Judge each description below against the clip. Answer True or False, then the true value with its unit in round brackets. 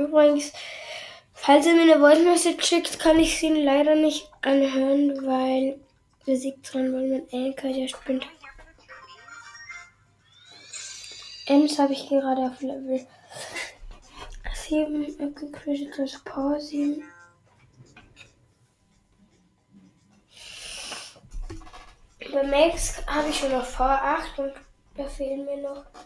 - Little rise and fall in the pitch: True (2.2 semitones)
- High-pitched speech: True (280 Hz)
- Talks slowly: True (95 wpm)